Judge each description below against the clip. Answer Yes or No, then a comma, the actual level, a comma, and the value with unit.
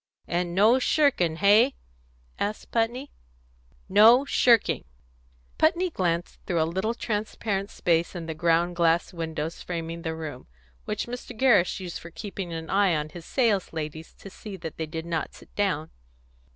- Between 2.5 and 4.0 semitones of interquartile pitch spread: No, average, 4.8 semitones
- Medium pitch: Yes, medium, 180 Hz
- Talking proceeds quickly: No, average, 155 wpm